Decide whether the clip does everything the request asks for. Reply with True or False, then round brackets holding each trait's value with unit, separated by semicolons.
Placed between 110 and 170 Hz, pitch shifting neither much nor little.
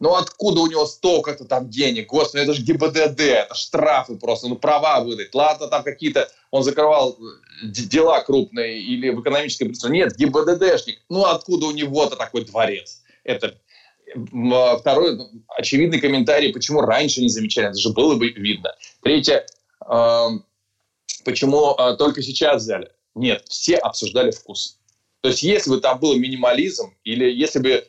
True (140 Hz; 4.1 semitones)